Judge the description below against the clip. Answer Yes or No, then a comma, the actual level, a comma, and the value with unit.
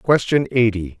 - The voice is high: No, low, 115 Hz